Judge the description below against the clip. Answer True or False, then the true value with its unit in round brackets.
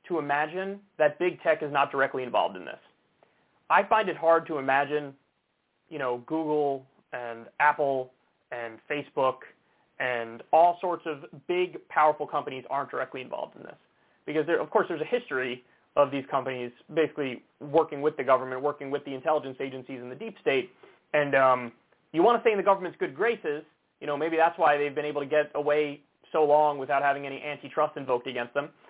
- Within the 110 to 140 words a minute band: False (185 wpm)